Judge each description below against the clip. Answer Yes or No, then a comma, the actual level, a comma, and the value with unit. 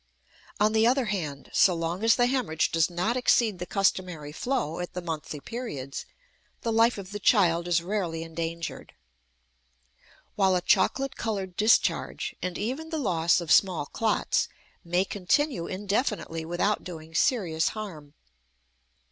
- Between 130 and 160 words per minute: Yes, average, 145 wpm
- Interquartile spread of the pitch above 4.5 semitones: Yes, average, 5.0 semitones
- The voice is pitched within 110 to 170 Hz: No, medium, 185 Hz